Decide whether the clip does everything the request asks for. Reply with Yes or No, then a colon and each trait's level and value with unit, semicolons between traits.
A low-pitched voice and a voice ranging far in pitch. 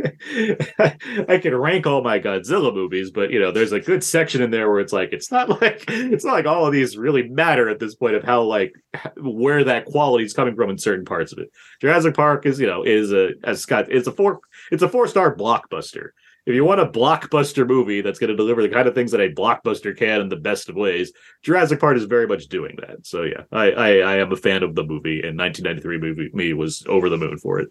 Yes: low, 130 Hz; wide, 7.7 semitones